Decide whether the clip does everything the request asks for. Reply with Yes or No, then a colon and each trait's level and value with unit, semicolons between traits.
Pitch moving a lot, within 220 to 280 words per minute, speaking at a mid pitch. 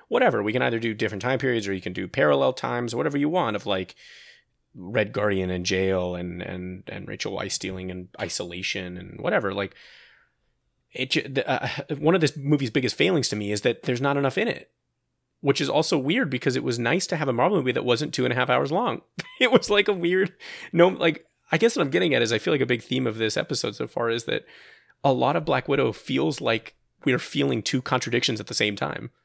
No: wide, 6.8 semitones; fast, 235 wpm; low, 120 Hz